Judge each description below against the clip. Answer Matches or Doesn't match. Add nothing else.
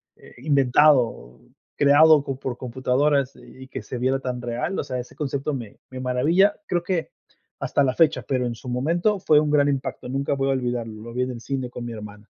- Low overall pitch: Matches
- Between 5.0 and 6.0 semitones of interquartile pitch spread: Doesn't match